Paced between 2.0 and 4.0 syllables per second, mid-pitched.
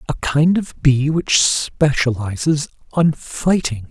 Yes: 3.5 syllables/s; medium, 145 Hz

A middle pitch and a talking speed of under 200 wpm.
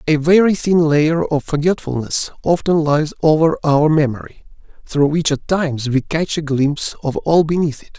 Yes: medium, 155 Hz; average, 175 wpm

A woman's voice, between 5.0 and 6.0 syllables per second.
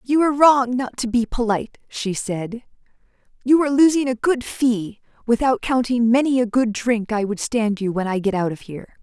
Yes: female; 5.2 syllables/s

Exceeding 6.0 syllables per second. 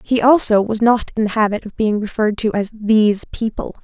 No: 5.5 syllables/s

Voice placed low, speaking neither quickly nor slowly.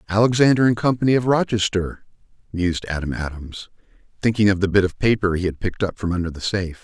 Yes: low, 100 Hz; average, 195 wpm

